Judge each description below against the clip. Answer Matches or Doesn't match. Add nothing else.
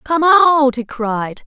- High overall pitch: Matches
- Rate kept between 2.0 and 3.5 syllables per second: Matches